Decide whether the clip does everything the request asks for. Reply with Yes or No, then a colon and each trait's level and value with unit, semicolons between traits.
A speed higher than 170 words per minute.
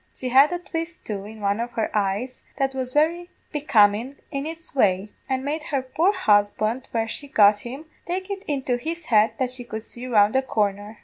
Yes: fast, 205 wpm